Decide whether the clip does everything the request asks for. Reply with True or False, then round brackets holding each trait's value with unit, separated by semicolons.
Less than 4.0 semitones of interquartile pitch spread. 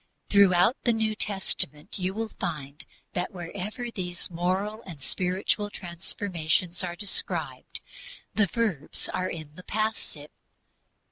True (3.4 semitones)